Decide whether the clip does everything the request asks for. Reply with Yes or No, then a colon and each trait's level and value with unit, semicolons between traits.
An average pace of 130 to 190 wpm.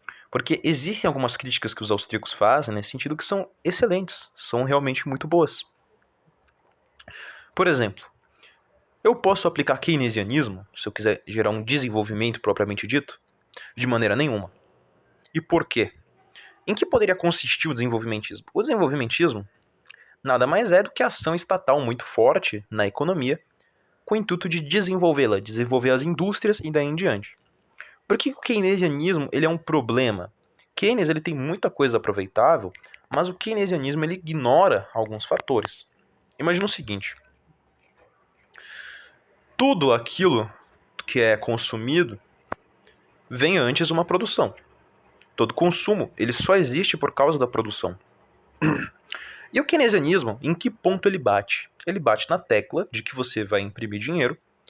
Yes: average, 145 wpm